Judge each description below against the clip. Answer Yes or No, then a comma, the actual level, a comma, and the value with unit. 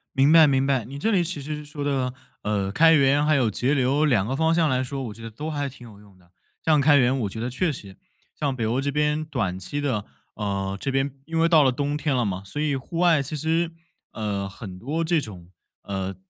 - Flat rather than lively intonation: No, wide, 5.6 semitones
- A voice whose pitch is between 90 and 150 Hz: Yes, low, 135 Hz